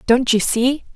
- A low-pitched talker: No, high, 245 Hz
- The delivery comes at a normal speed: Yes, average, 190 wpm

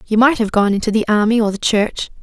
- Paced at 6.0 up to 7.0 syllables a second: Yes, 6.1 syllables/s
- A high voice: Yes, high, 220 Hz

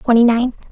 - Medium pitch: No, high, 240 Hz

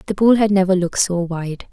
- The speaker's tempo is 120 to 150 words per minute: No, fast, 245 wpm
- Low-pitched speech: No, high, 190 Hz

